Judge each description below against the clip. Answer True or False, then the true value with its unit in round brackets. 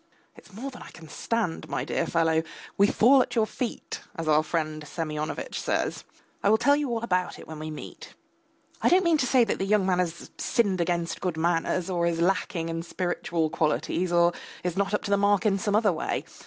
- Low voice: False (180 Hz)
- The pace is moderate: False (220 wpm)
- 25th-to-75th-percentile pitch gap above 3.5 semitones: True (4.3 semitones)